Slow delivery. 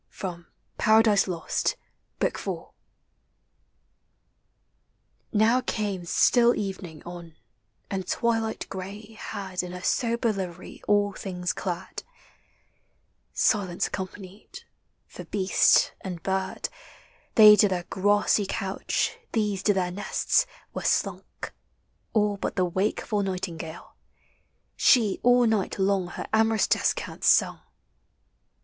Yes: slow, 105 wpm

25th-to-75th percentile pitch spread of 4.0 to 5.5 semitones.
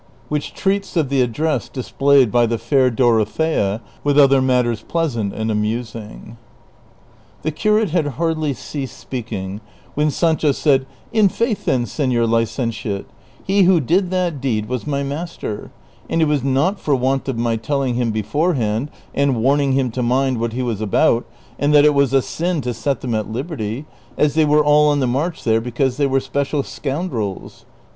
Yes: average, 4.3 semitones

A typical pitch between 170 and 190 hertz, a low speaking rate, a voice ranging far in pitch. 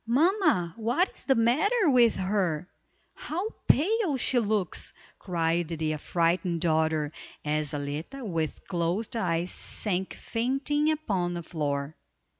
Yes: medium, 185 Hz; slow, 120 wpm; wide, 8.2 semitones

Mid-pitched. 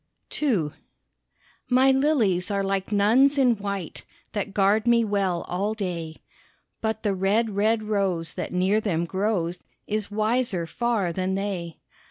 No: high, 200 Hz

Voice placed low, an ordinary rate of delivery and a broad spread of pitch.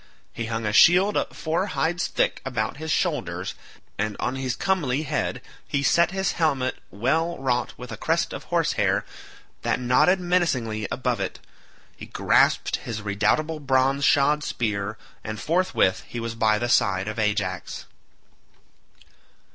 Yes: low, 125 Hz; average, 145 wpm; wide, 6.6 semitones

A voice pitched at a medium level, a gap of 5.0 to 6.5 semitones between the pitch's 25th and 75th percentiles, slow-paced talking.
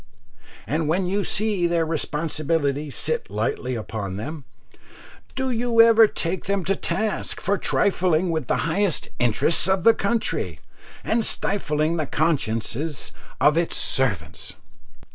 Yes: medium, 165 Hz; wide, 5.4 semitones; slow, 130 wpm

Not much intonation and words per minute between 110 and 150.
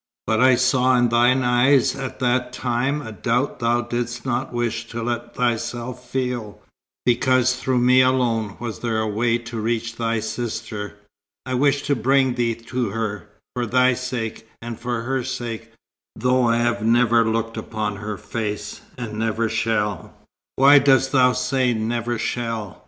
No: narrow, 2.0 semitones; average, 165 wpm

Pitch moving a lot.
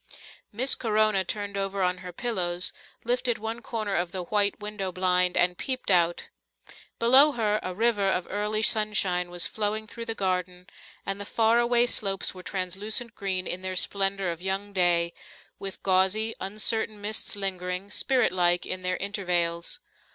No: average, 3.0 semitones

